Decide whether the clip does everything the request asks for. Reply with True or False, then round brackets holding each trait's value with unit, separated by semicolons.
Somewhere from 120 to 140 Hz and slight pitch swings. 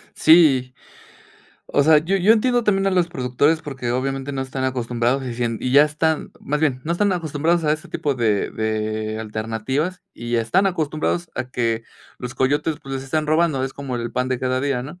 False (135 Hz; 4.4 semitones)